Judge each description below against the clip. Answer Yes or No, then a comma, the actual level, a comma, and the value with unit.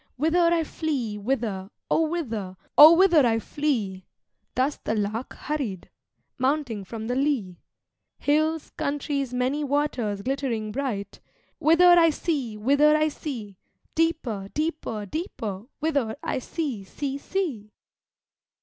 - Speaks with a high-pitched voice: Yes, very high, 270 Hz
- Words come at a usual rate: No, slow, 120 wpm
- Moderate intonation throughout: No, wide, 6.0 semitones